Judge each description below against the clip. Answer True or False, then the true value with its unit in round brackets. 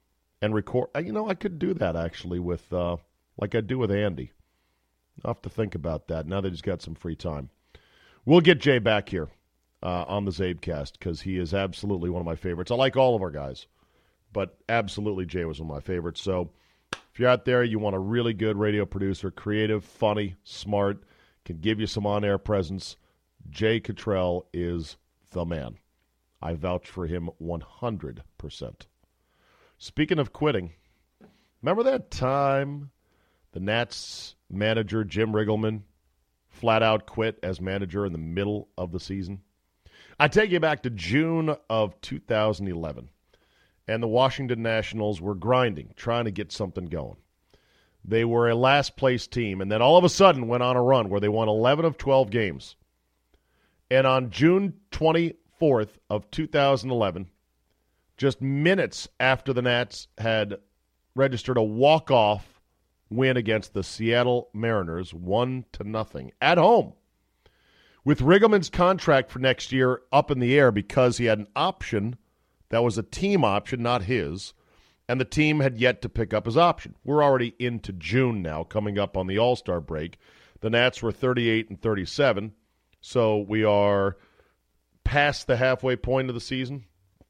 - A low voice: True (105 Hz)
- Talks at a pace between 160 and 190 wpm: True (165 wpm)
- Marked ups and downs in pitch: True (5.7 semitones)